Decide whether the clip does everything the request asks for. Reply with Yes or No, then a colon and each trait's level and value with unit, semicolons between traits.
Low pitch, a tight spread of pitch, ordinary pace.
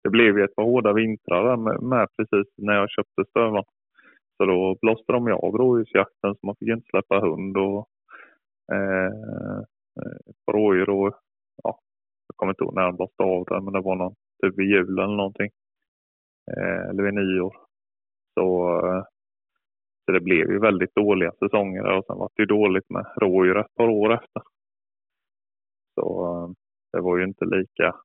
Yes: very low, 95 Hz; narrow, 2.3 semitones; average, 180 wpm